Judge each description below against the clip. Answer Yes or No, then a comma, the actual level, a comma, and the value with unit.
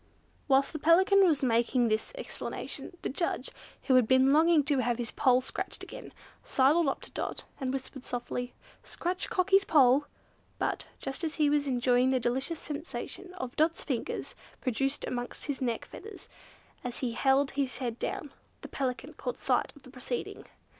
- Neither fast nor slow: Yes, average, 165 wpm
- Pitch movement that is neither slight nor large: Yes, average, 3.8 semitones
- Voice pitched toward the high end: Yes, very high, 270 Hz